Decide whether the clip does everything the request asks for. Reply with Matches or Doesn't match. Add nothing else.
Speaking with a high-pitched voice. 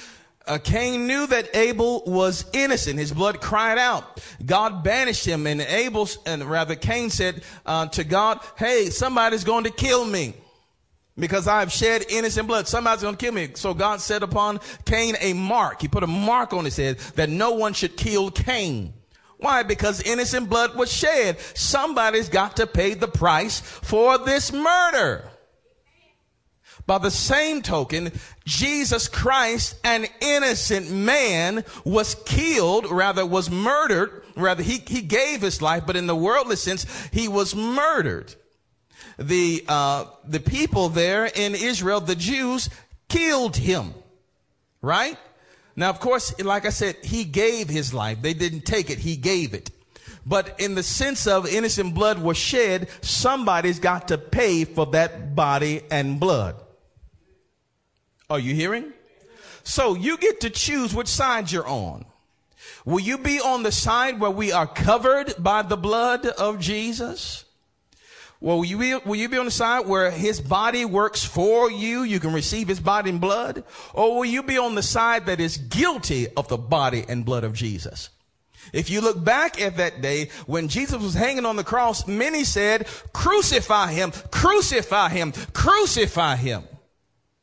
Matches